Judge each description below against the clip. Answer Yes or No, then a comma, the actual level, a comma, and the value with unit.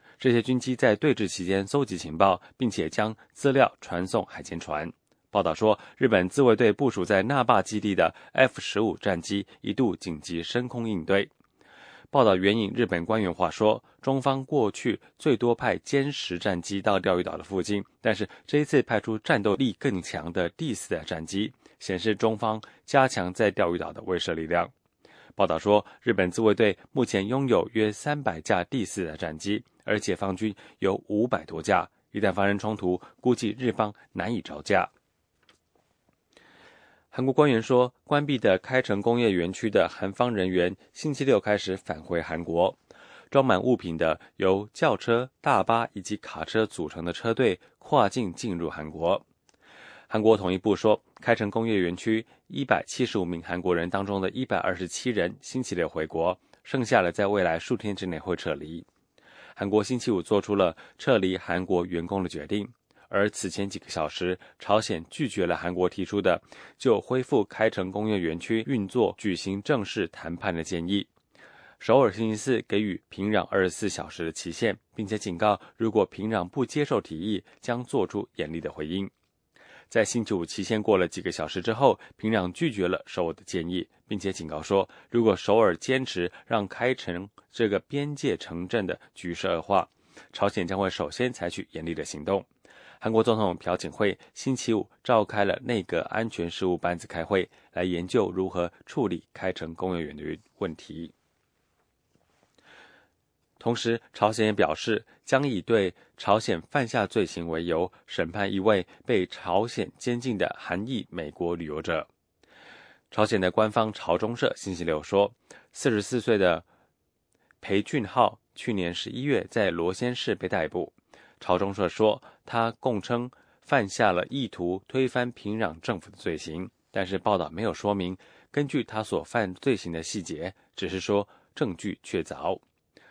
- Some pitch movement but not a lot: Yes, average, 4.5 semitones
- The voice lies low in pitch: Yes, low, 100 Hz